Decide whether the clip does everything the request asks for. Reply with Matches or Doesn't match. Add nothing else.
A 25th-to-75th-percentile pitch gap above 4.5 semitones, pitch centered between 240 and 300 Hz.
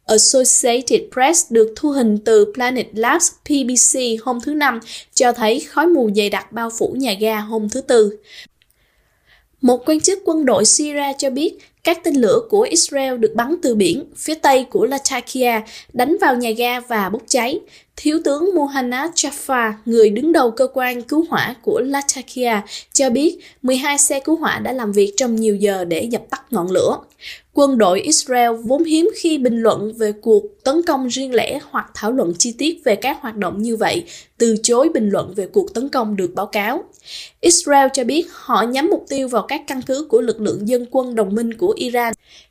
Matches